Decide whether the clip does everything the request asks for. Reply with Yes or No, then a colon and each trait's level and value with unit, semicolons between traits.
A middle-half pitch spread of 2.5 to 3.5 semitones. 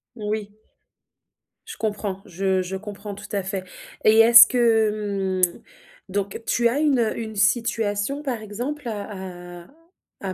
Yes: average, 2.9 semitones